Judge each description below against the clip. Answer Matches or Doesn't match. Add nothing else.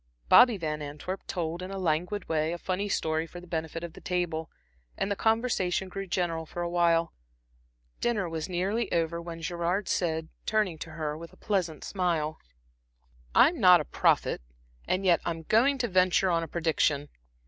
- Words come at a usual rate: Matches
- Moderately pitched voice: Matches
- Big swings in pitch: Doesn't match